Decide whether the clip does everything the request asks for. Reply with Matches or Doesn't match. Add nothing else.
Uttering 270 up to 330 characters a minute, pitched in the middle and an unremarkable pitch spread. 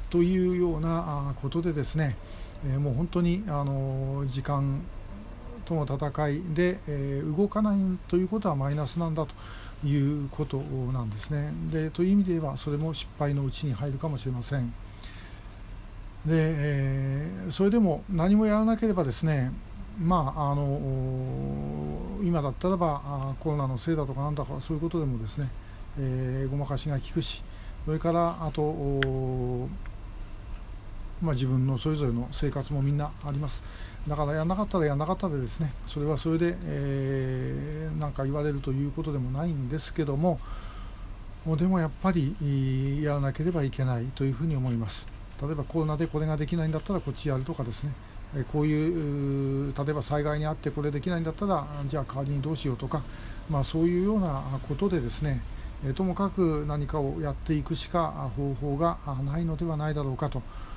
Doesn't match